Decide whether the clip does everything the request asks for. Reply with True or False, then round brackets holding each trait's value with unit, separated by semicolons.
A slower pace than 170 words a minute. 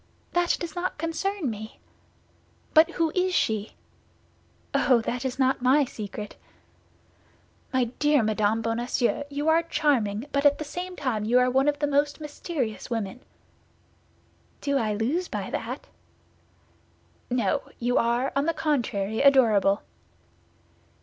True (135 wpm)